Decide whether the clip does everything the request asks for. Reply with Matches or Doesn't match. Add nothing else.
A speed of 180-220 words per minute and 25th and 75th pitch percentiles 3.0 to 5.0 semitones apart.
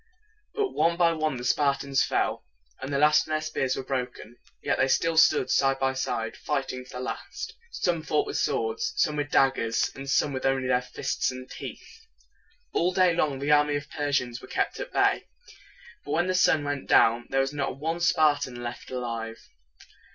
Matches